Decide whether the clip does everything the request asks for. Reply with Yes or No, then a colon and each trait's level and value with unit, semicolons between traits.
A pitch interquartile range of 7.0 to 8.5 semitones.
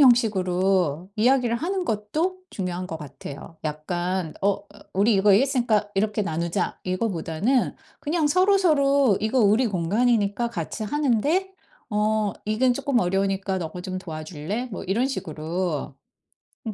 No: wide, 5.5 semitones